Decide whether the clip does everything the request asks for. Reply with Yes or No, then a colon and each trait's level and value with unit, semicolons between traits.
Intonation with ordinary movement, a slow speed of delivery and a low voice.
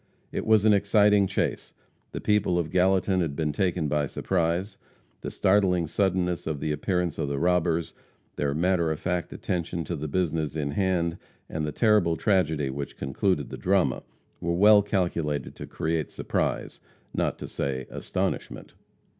No: average, 3.7 semitones; average, 160 wpm; very low, 85 Hz